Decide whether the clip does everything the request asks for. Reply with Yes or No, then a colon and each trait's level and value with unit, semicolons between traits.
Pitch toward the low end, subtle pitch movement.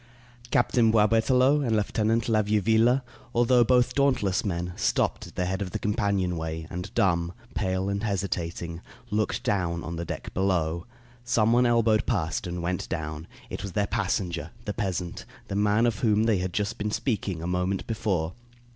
No: low, 100 Hz; average, 4.0 semitones